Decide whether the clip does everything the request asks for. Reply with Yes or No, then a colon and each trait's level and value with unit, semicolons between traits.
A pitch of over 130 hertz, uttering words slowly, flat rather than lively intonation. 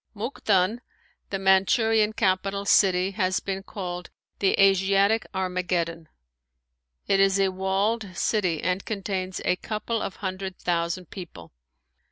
Yes: high, 190 Hz; slow, 120 wpm; narrow, 1.6 semitones